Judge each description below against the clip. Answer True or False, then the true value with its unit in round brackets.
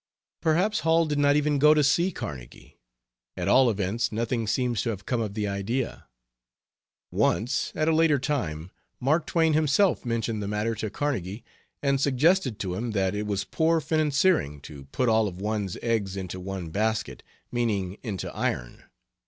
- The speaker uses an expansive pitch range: True (6.8 semitones)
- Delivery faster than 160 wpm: True (170 wpm)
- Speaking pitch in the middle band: False (115 Hz)